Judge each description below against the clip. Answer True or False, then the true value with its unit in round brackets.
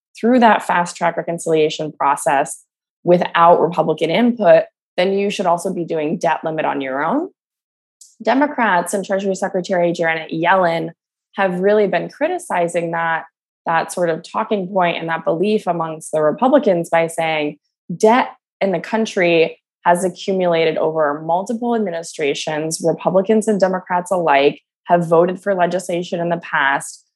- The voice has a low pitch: False (175 Hz)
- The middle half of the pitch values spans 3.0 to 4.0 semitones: True (3.4 semitones)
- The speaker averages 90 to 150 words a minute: True (140 wpm)